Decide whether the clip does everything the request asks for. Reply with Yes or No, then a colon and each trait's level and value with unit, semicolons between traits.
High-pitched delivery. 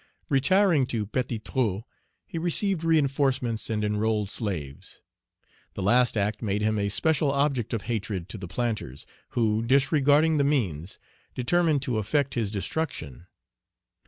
No: low, 120 Hz